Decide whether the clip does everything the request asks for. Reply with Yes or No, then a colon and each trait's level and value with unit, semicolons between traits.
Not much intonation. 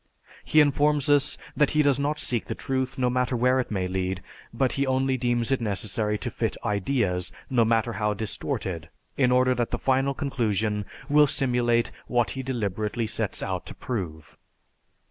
No: average, 4.1 semitones